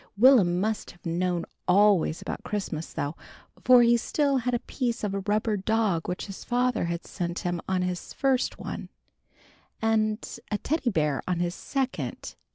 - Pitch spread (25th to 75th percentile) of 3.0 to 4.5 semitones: No, average, 5.1 semitones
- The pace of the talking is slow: No, average, 165 wpm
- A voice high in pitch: Yes, high, 205 Hz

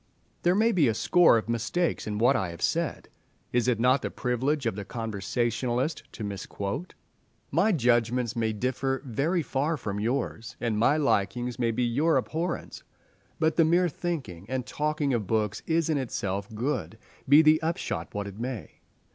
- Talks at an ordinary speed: Yes, average, 170 wpm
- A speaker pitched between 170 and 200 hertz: No, low, 125 Hz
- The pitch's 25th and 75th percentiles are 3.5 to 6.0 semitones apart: Yes, wide, 5.5 semitones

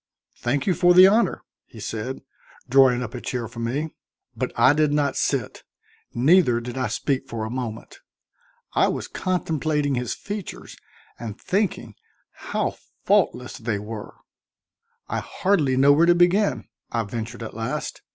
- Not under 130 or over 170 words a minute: Yes, average, 150 wpm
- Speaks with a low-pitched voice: Yes, low, 130 Hz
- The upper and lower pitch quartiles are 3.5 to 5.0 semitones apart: No, wide, 5.5 semitones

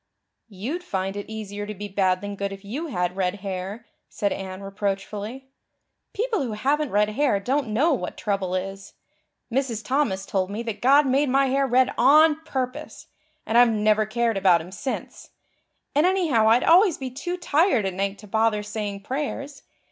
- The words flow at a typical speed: Yes, average, 180 wpm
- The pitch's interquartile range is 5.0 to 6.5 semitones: Yes, wide, 5.5 semitones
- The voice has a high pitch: Yes, high, 220 Hz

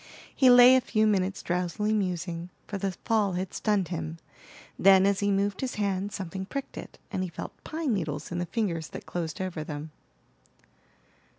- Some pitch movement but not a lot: Yes, average, 3.2 semitones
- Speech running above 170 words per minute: Yes, average, 180 wpm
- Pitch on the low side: No, high, 190 Hz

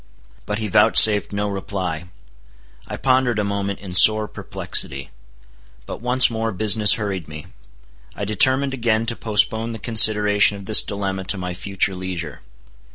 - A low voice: Yes, low, 105 Hz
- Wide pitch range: No, narrow, 2.5 semitones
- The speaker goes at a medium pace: Yes, average, 150 wpm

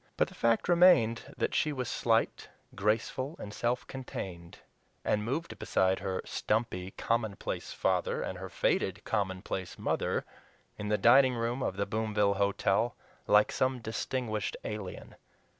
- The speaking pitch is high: No, low, 110 Hz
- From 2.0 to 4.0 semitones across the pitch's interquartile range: Yes, average, 3.5 semitones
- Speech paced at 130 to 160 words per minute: Yes, average, 140 wpm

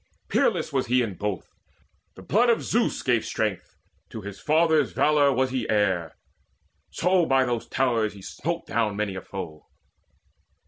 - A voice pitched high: No, low, 120 Hz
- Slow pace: No, average, 155 wpm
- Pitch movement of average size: No, wide, 6.1 semitones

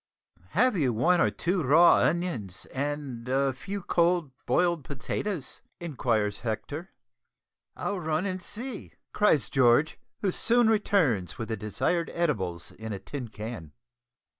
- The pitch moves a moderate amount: No, wide, 7.5 semitones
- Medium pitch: Yes, medium, 145 Hz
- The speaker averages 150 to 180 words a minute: No, slow, 135 wpm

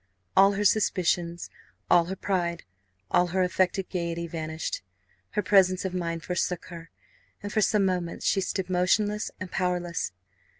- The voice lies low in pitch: No, medium, 180 Hz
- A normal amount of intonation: No, narrow, 2.1 semitones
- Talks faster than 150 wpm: No, average, 145 wpm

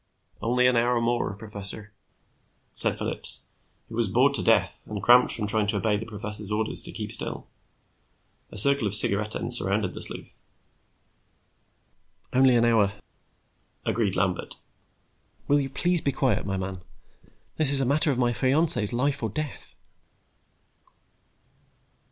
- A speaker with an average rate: Yes, average, 145 wpm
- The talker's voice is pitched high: No, low, 115 Hz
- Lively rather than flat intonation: No, average, 4.0 semitones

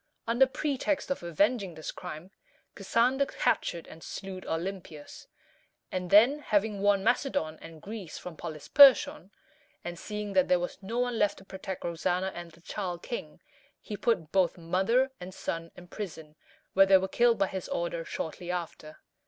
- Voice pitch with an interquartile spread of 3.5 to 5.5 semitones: Yes, average, 4.5 semitones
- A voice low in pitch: No, high, 190 Hz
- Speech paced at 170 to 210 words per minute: No, average, 160 wpm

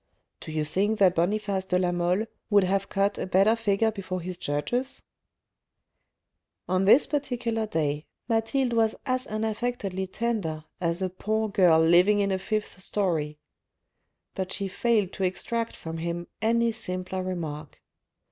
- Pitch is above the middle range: Yes, high, 195 Hz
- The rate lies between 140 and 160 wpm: Yes, average, 150 wpm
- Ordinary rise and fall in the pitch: Yes, average, 3.7 semitones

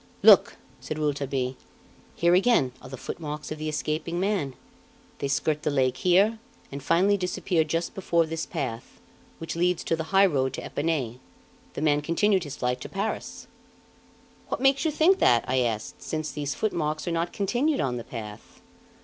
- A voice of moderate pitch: Yes, medium, 155 Hz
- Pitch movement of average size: Yes, average, 4.9 semitones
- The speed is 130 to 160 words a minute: No, average, 175 wpm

